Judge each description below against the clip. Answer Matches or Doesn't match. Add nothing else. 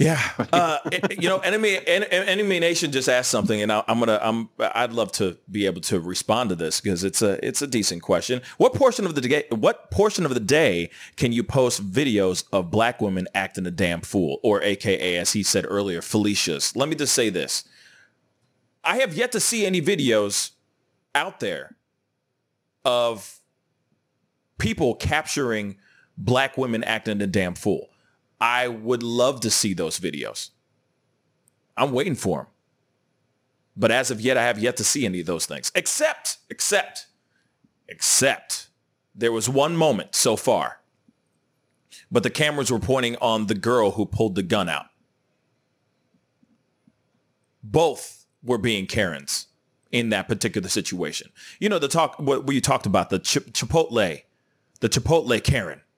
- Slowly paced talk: Doesn't match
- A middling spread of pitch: Matches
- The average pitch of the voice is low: Matches